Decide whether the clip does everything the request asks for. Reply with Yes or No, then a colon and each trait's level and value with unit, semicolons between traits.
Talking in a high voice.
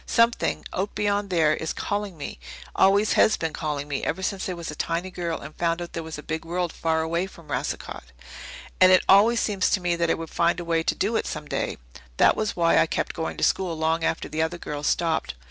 No: medium, 170 Hz